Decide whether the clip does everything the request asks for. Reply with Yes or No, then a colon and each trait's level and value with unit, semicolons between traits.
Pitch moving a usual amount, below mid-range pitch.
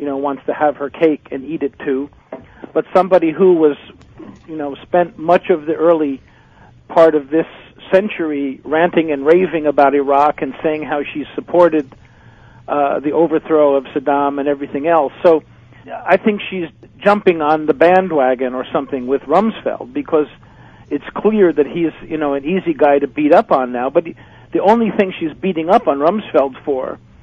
No: average, 3.4 semitones; medium, 155 Hz